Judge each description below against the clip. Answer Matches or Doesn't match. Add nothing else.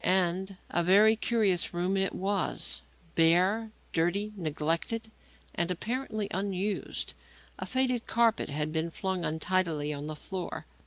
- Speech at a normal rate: Doesn't match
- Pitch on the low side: Doesn't match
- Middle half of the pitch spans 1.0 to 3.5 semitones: Doesn't match